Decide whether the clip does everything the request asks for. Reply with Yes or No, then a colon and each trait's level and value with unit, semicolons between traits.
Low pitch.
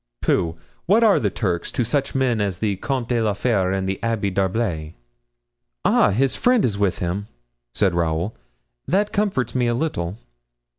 Yes: low, 105 Hz